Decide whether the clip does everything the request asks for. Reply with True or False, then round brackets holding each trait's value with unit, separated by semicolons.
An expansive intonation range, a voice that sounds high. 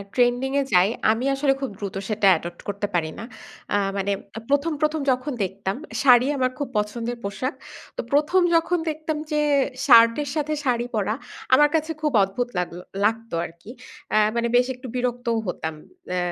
True (5.7 semitones; 245 Hz)